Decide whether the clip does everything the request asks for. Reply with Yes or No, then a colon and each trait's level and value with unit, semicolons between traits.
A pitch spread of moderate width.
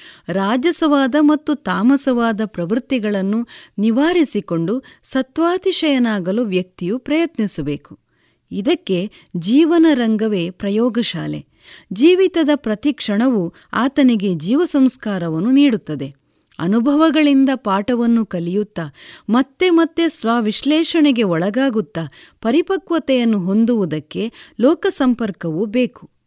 No: wide, 6.9 semitones